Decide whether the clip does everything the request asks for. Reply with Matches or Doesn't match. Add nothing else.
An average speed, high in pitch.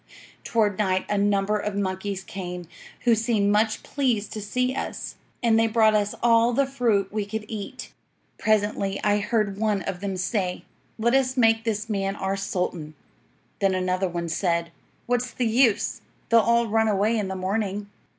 Matches